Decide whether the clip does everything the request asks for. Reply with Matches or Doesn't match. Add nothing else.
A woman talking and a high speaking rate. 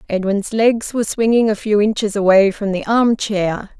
Doesn't match